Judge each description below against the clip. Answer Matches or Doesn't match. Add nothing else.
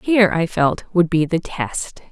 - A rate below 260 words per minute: Matches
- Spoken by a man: Doesn't match